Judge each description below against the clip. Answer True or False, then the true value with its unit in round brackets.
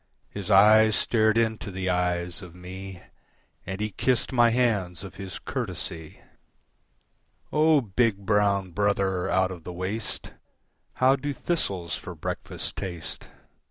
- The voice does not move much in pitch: False (3.4 semitones)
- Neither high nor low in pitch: False (100 Hz)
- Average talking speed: False (130 wpm)